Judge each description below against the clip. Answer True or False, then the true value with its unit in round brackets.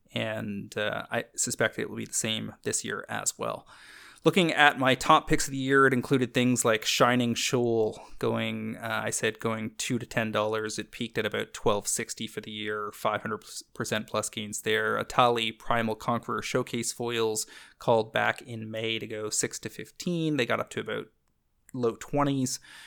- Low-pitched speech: True (115 Hz)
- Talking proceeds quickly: False (185 wpm)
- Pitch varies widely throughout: False (2.6 semitones)